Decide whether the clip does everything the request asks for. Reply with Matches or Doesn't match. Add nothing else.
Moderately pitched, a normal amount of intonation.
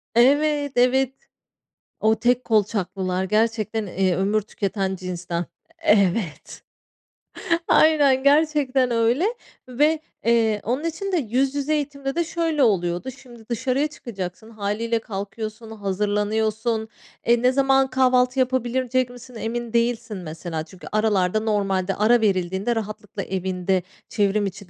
Doesn't match